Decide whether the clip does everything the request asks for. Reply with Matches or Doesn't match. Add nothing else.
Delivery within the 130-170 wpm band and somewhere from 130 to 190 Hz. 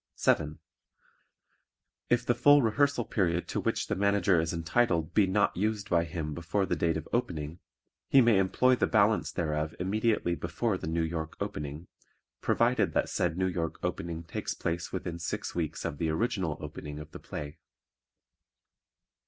Doesn't match